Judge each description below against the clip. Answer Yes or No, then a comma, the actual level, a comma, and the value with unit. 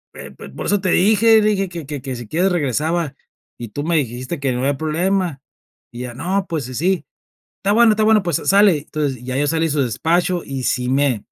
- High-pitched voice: No, medium, 160 Hz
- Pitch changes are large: Yes, wide, 6.0 semitones